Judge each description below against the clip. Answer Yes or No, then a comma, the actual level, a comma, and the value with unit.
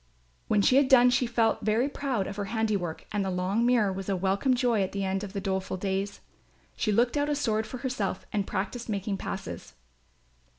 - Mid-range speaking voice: No, high, 210 Hz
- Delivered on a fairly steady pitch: No, average, 3.9 semitones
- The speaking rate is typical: No, fast, 210 wpm